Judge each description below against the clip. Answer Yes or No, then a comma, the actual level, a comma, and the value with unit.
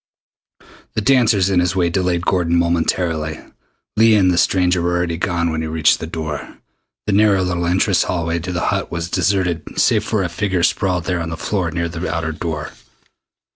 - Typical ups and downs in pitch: No, narrow, 2.1 semitones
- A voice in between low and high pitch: No, very low, 85 Hz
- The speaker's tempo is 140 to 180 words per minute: No, average, 190 wpm